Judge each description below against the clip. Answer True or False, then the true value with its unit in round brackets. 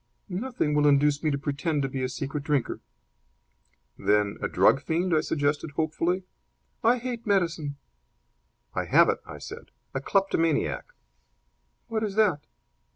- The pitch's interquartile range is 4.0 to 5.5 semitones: True (4.8 semitones)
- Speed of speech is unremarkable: True (145 wpm)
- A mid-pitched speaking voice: True (155 Hz)